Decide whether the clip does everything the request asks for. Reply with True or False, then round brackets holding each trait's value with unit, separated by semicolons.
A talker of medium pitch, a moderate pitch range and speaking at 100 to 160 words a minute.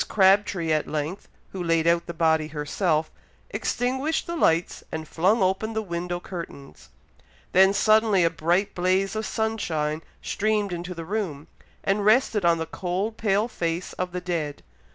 True (180 Hz; 4.0 semitones; 155 wpm)